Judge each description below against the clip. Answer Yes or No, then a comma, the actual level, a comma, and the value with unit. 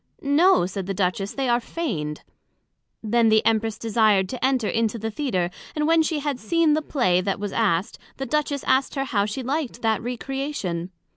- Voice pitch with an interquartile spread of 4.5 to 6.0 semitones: Yes, wide, 5.4 semitones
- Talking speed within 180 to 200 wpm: Yes, average, 190 wpm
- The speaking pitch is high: Yes, high, 230 Hz